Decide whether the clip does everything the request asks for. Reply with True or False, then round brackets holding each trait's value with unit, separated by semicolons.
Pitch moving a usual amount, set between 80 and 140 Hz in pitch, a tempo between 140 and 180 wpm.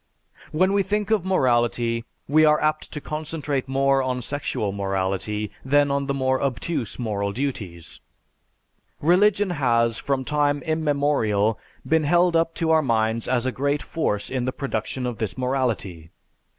True (4.8 semitones; 135 Hz; 150 wpm)